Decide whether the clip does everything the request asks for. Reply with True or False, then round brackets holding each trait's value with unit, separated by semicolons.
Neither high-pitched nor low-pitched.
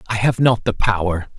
False (105 Hz)